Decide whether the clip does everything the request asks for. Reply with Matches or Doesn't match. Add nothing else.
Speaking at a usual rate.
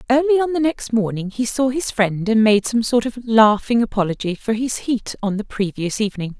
Doesn't match